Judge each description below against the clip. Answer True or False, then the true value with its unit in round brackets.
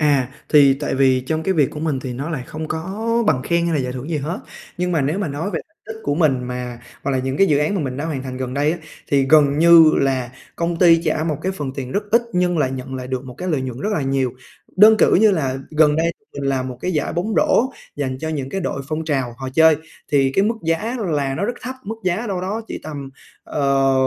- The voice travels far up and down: False (4.2 semitones)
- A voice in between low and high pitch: True (150 Hz)